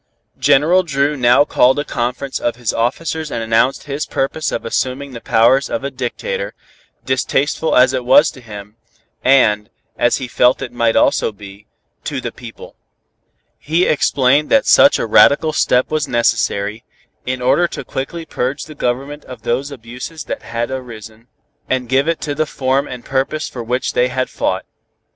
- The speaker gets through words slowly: No, average, 170 wpm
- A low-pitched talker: Yes, low, 130 Hz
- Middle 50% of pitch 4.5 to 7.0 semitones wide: No, average, 3.3 semitones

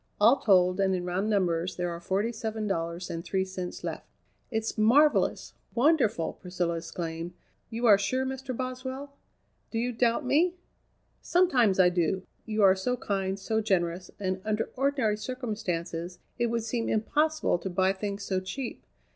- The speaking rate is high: No, average, 160 wpm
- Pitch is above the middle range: Yes, high, 205 Hz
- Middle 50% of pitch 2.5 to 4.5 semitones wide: No, average, 5.1 semitones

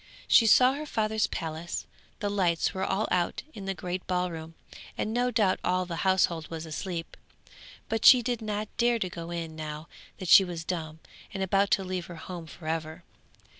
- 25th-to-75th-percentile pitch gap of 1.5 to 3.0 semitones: No, average, 3.9 semitones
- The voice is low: No, medium, 180 Hz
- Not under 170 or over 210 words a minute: Yes, average, 190 wpm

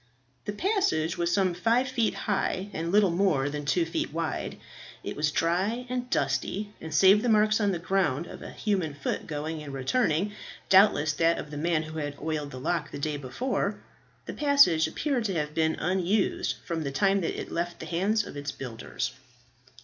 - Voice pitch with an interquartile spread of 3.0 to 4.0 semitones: No, average, 5.2 semitones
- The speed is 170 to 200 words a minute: Yes, average, 195 wpm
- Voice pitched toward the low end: No, medium, 170 Hz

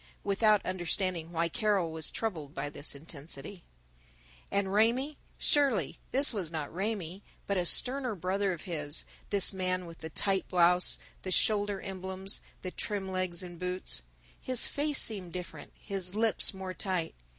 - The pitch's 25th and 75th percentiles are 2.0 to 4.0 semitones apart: Yes, average, 3.2 semitones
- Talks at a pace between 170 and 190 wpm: No, average, 150 wpm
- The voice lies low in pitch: No, medium, 185 Hz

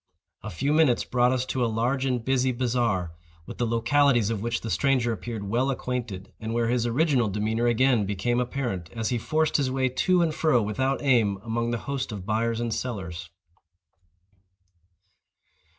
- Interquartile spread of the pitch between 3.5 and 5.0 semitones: No, average, 2.9 semitones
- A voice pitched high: No, low, 120 Hz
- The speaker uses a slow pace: No, average, 175 wpm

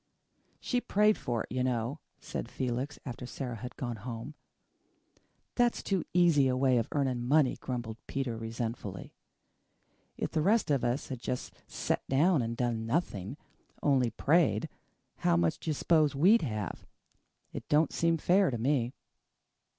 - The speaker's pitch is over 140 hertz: No, low, 130 Hz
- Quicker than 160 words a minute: No, average, 155 wpm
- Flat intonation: No, average, 4.7 semitones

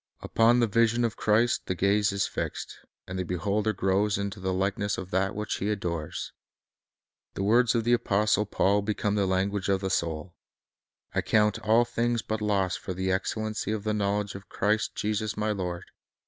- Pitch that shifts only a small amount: Yes, narrow, 2.1 semitones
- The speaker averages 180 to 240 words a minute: Yes, average, 185 wpm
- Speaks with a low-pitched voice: Yes, low, 105 Hz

